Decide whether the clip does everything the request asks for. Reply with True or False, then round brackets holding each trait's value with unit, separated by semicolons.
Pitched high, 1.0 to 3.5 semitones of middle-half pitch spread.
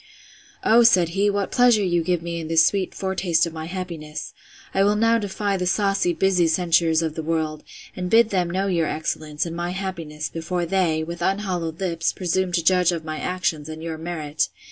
False (175 Hz; 2.8 semitones)